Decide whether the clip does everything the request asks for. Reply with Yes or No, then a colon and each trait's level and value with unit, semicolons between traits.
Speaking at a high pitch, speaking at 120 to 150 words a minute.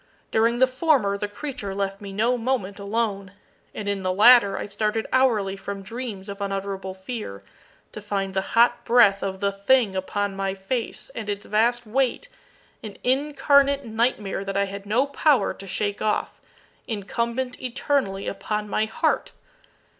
No: high, 210 Hz; average, 160 wpm